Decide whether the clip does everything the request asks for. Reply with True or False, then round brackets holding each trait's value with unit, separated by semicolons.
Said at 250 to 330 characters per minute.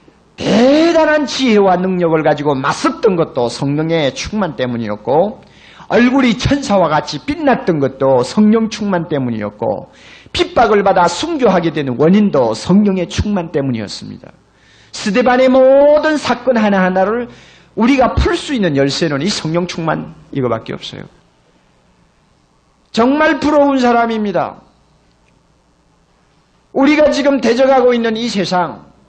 True (275 characters per minute)